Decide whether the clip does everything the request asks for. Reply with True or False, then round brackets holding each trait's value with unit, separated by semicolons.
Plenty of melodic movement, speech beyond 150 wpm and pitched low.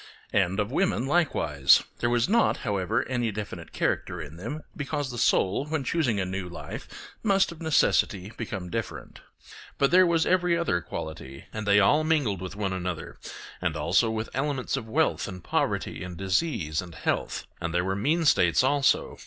True (8.2 semitones; 180 wpm; 110 Hz)